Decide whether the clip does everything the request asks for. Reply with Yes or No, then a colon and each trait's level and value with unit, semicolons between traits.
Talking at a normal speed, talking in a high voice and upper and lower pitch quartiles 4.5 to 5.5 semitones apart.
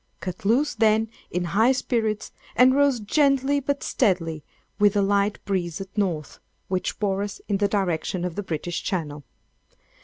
No: average, 160 wpm; high, 205 Hz; average, 4.0 semitones